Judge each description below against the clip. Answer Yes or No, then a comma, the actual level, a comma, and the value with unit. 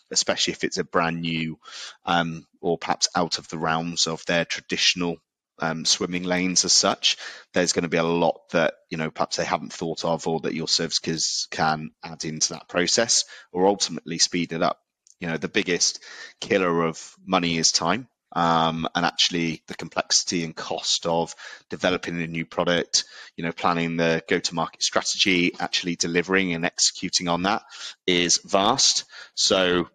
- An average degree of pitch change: No, narrow, 1.3 semitones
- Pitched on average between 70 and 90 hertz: Yes, very low, 85 Hz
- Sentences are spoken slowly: No, average, 175 wpm